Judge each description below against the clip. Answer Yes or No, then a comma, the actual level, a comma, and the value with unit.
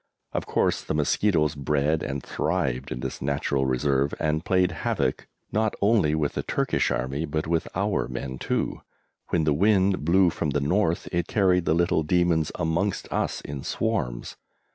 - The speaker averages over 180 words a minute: No, average, 165 wpm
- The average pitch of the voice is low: Yes, very low, 80 Hz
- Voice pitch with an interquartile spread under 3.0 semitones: No, average, 4.4 semitones